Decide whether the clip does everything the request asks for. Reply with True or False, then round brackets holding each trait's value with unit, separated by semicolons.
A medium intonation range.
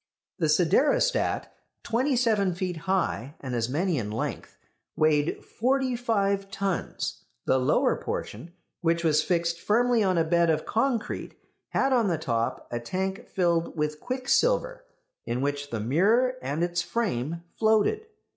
False (7.1 semitones)